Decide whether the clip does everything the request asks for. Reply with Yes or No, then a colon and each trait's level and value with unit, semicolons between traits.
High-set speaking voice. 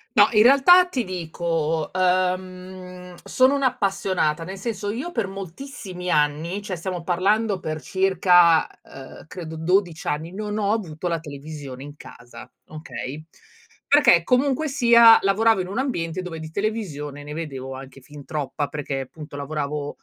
No: medium, 180 Hz